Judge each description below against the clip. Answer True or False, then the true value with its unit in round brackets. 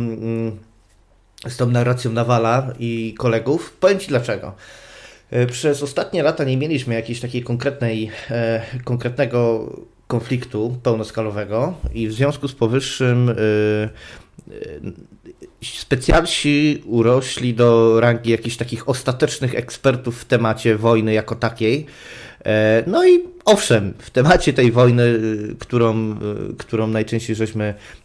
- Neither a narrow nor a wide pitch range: False (2.1 semitones)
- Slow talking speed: True (105 wpm)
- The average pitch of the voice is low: True (120 Hz)